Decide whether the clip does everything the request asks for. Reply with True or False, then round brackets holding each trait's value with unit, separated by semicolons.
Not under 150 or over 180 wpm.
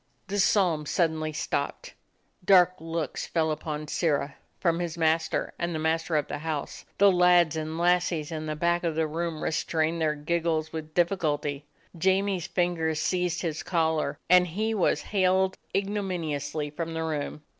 True (160 wpm)